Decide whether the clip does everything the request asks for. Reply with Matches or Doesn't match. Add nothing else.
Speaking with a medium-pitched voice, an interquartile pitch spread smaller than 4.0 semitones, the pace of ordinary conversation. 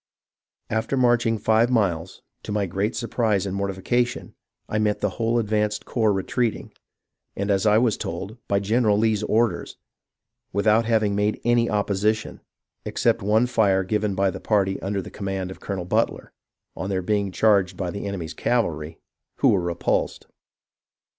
Doesn't match